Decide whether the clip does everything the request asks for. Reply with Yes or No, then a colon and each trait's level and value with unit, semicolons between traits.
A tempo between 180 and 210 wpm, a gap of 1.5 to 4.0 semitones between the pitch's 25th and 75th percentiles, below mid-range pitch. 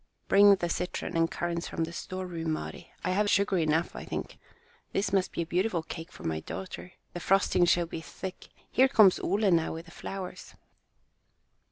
No: average, 185 wpm; average, 2.7 semitones; medium, 180 Hz